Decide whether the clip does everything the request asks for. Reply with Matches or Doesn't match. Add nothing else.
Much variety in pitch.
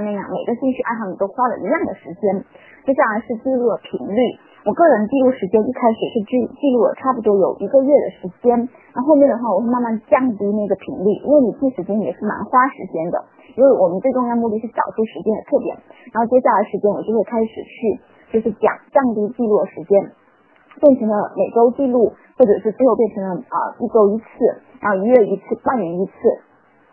Doesn't match